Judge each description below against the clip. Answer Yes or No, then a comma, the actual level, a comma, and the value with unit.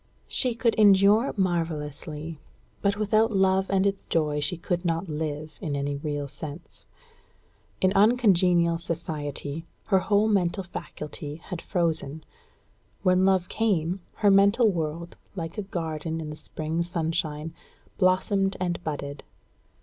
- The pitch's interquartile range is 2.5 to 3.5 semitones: No, average, 3.9 semitones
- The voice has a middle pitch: Yes, medium, 170 Hz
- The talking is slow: Yes, slow, 130 wpm